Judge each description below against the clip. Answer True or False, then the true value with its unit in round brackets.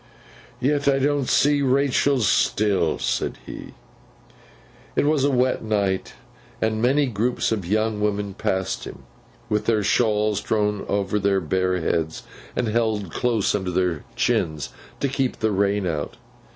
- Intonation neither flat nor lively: True (4.4 semitones)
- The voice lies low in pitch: True (105 Hz)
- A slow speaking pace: False (145 wpm)